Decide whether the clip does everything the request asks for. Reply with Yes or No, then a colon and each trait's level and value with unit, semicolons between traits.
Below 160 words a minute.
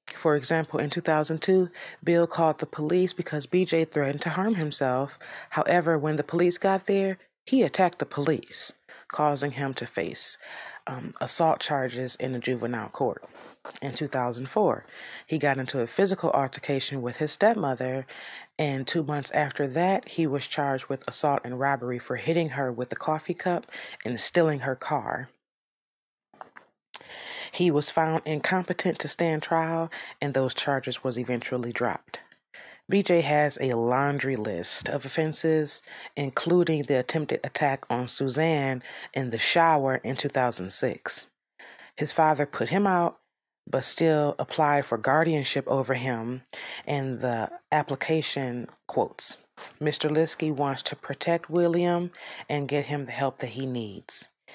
Yes: average, 145 wpm